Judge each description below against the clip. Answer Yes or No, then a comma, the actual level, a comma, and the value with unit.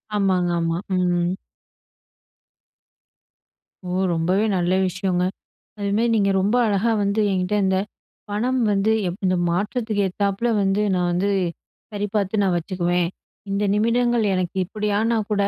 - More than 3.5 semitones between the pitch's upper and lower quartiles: No, narrow, 2.6 semitones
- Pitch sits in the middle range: No, high, 200 Hz